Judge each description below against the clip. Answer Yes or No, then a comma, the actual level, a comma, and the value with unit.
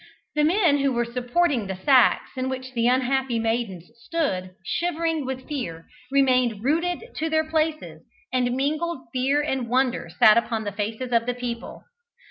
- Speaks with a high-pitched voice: Yes, very high, 255 Hz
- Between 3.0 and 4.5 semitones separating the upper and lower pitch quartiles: Yes, average, 4.2 semitones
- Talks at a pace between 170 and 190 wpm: No, average, 160 wpm